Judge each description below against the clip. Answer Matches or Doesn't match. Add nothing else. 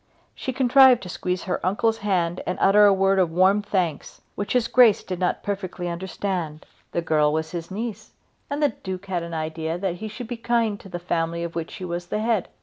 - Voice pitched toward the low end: Doesn't match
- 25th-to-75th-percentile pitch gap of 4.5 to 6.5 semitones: Doesn't match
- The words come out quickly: Matches